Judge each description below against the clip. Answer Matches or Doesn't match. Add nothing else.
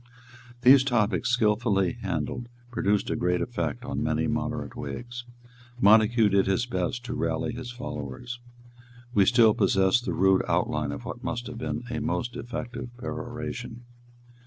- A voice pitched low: Matches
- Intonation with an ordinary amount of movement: Matches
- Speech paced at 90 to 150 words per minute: Matches